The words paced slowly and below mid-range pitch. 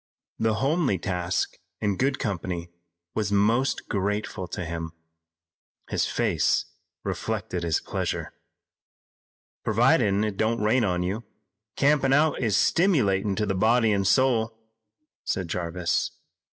Yes: slow, 120 wpm; low, 105 Hz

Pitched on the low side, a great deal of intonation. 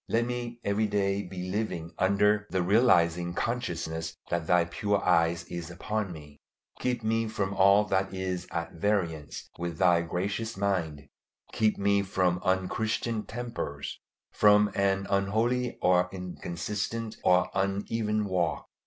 No: very low, 95 Hz; average, 3.4 semitones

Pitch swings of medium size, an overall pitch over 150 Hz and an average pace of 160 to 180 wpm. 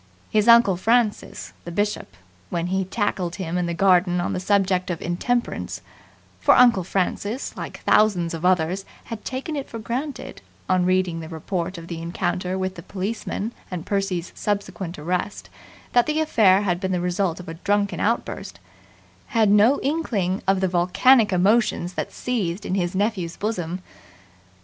Yes: average, 3.3 semitones; high, 190 Hz; average, 165 wpm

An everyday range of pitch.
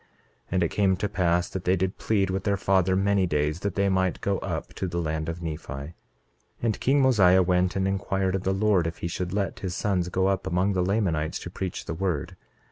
No: narrow, 2.0 semitones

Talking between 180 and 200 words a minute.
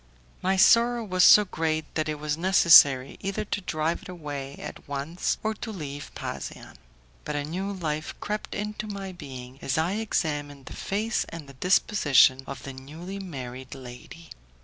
No: average, 170 wpm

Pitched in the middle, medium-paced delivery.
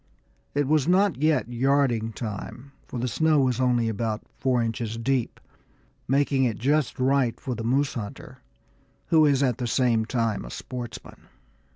No: low, 125 Hz; average, 165 wpm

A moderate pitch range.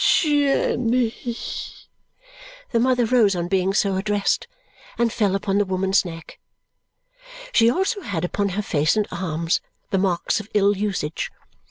Yes: average, 3.7 semitones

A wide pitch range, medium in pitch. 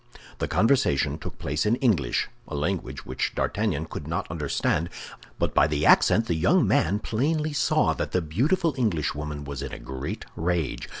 No: wide, 7.6 semitones; very low, 85 Hz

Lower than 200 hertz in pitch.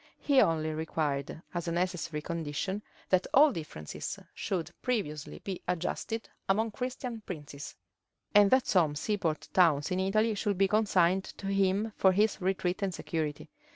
Yes: medium, 185 Hz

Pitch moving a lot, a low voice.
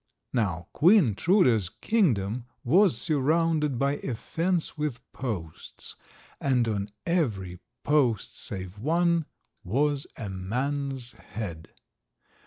Yes: wide, 7.1 semitones; low, 130 Hz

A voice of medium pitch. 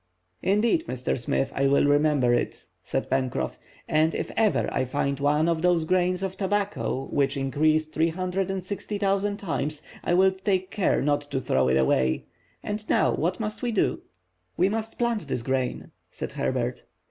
Yes: medium, 165 Hz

